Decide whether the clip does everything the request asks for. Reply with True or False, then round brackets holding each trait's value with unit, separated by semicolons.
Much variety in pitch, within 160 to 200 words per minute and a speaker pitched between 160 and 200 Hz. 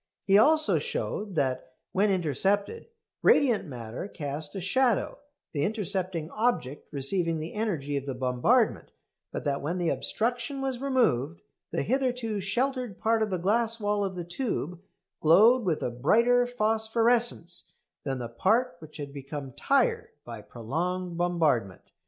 False (7.8 semitones; 145 wpm; 185 Hz)